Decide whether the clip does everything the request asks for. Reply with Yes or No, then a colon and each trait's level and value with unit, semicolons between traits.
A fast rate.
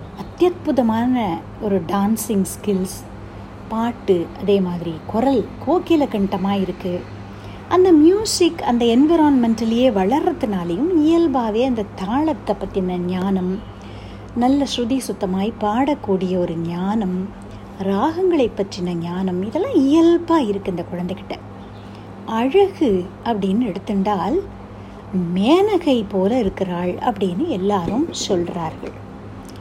No: average, 90 wpm